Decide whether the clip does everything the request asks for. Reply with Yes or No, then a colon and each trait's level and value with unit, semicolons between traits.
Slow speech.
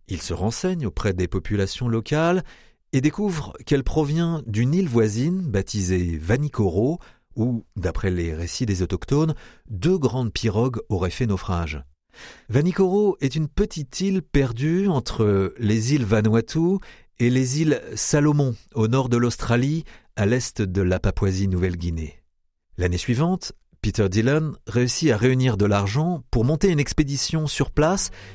Yes: slow, 140 wpm